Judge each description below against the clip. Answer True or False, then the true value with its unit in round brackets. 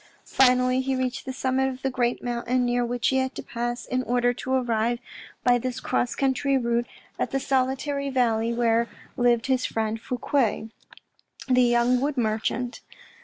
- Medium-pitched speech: False (250 Hz)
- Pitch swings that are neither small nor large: False (1.6 semitones)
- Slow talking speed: False (170 wpm)